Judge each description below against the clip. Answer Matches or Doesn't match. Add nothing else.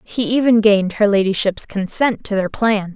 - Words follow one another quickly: Doesn't match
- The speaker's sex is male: Doesn't match